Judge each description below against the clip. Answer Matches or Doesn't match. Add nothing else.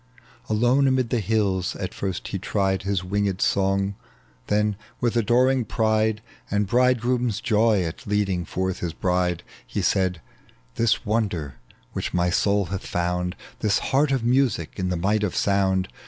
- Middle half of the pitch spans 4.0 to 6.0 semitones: Doesn't match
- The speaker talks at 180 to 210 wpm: Doesn't match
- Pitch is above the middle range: Doesn't match